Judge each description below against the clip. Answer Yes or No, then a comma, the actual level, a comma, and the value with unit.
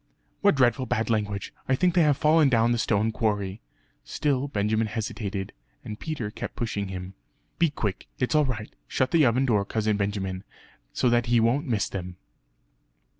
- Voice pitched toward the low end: Yes, low, 115 Hz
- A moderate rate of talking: Yes, average, 175 wpm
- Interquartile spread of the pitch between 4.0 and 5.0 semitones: Yes, average, 4.4 semitones